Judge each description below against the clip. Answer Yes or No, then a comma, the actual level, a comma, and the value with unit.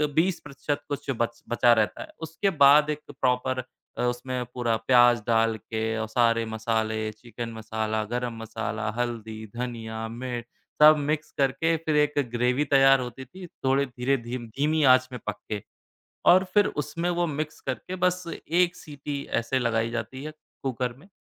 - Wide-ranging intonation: No, average, 4.2 semitones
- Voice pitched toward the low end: Yes, low, 125 Hz